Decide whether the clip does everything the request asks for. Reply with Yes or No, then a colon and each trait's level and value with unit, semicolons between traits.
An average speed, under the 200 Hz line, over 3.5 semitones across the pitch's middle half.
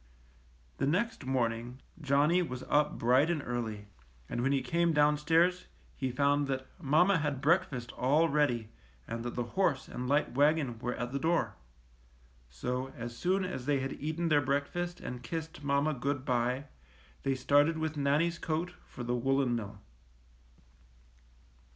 Yes: average, 155 wpm; medium, 140 Hz; average, 4.1 semitones